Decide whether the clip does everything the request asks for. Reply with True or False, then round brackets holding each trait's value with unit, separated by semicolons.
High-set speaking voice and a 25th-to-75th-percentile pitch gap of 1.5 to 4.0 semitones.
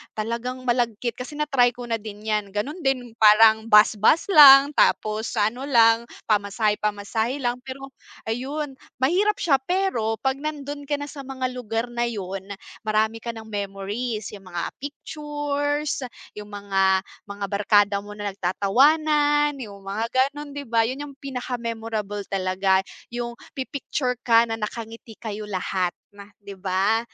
False (230 Hz; 4.6 semitones)